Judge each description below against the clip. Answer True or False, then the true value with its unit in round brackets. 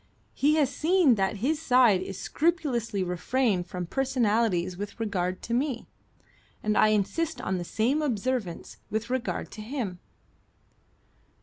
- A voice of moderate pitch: False (225 Hz)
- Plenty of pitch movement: True (5.7 semitones)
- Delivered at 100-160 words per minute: True (135 wpm)